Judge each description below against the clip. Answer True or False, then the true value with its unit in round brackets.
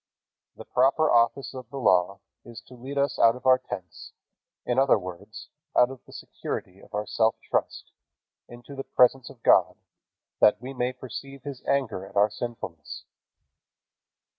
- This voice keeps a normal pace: True (165 wpm)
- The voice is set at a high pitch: False (125 Hz)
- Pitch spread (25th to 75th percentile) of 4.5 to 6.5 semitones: False (4.1 semitones)